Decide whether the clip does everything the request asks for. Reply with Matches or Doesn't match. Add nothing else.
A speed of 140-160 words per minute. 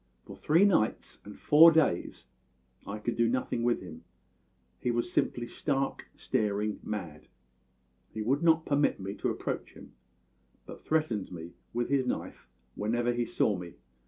Matches